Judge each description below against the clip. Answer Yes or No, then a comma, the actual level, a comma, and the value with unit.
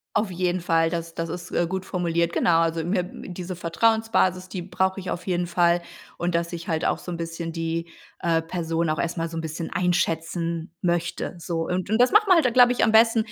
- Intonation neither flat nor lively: No, narrow, 1.9 semitones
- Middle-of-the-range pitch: Yes, medium, 175 Hz